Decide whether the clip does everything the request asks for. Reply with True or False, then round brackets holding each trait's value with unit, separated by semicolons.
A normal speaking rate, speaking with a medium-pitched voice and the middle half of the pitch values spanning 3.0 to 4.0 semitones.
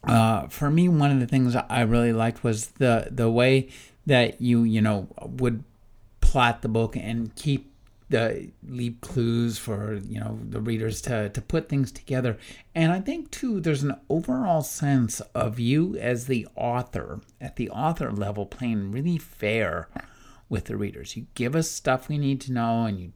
False (180 wpm; 120 Hz; 3.4 semitones)